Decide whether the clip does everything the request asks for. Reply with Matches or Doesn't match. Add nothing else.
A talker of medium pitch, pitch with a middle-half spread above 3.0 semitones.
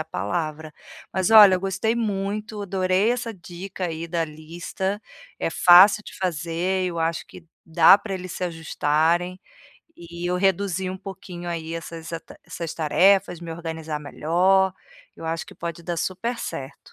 Doesn't match